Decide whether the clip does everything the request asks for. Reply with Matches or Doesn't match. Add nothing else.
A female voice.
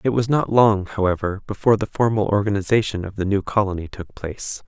Doesn't match